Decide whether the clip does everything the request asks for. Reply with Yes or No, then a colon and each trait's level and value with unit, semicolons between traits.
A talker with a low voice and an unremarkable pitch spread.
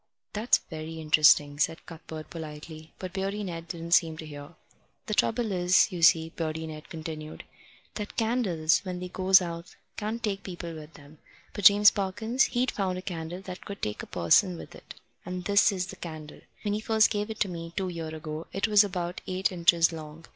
No: medium, 175 Hz; average, 3.8 semitones